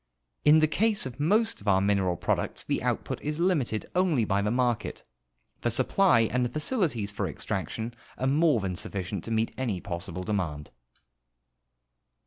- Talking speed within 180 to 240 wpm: No, average, 160 wpm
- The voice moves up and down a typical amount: No, wide, 7.3 semitones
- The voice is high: No, low, 115 Hz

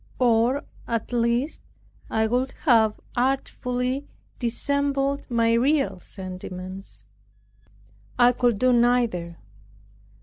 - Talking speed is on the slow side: Yes, slow, 90 wpm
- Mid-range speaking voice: No, high, 240 Hz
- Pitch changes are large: No, average, 2.7 semitones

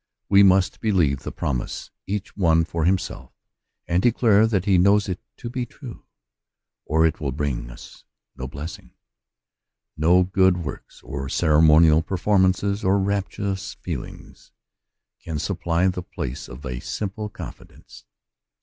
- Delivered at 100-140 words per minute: Yes, slow, 135 wpm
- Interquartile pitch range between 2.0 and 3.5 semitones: No, average, 4.2 semitones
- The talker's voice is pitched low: Yes, very low, 90 Hz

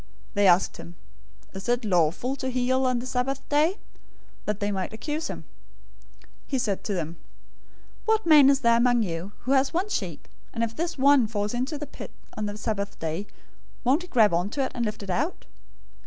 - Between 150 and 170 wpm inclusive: No, average, 200 wpm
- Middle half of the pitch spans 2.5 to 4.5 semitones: No, average, 5.2 semitones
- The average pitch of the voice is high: Yes, high, 240 Hz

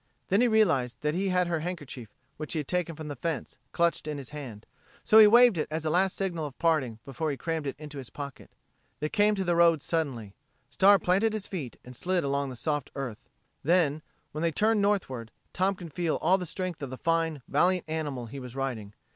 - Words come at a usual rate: No, fast, 220 wpm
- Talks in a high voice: No, medium, 160 Hz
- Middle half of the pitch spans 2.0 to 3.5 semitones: No, average, 4.7 semitones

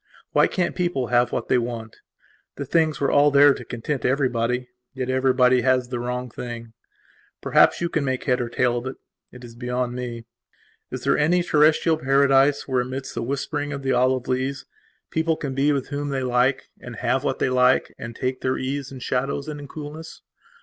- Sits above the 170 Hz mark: No, low, 130 Hz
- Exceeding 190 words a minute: Yes, average, 200 wpm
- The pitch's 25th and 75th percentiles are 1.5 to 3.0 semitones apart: Yes, narrow, 2.4 semitones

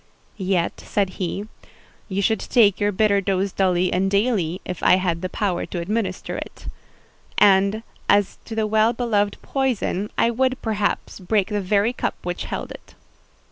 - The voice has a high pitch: Yes, high, 200 Hz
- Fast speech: No, average, 165 wpm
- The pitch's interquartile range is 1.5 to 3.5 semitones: Yes, average, 2.9 semitones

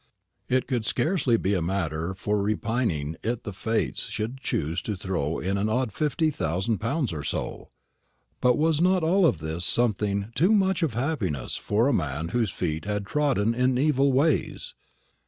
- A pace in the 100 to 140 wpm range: No, average, 170 wpm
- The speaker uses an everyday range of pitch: No, wide, 6.7 semitones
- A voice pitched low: Yes, low, 110 Hz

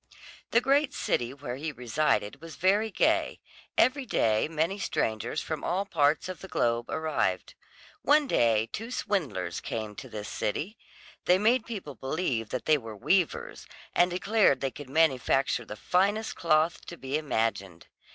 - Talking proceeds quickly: No, average, 155 wpm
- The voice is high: No, medium, 155 Hz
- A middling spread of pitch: No, wide, 8.0 semitones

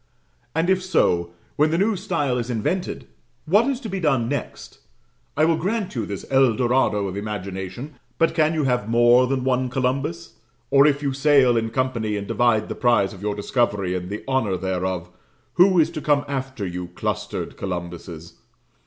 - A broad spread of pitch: Yes, wide, 6.8 semitones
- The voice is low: Yes, low, 125 Hz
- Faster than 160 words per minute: Yes, average, 180 wpm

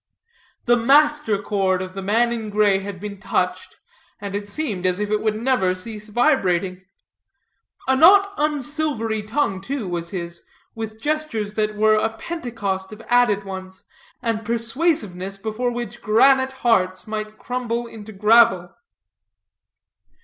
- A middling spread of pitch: Yes, average, 3.7 semitones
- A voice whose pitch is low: No, high, 215 Hz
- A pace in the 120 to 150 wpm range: Yes, average, 140 wpm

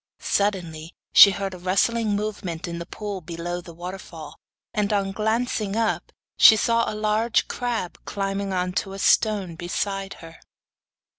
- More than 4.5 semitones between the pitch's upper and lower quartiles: No, average, 3.2 semitones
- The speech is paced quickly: No, average, 150 wpm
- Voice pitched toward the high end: Yes, high, 195 Hz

